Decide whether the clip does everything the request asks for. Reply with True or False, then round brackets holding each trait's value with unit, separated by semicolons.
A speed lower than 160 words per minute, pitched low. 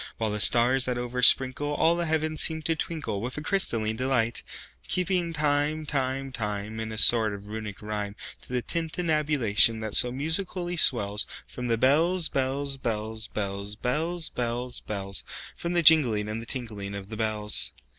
True (140 wpm; 125 Hz)